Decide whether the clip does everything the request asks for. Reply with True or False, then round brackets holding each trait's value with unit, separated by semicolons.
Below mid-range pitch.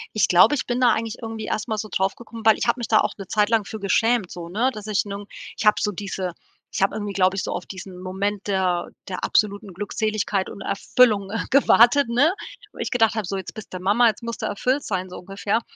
False (210 Hz)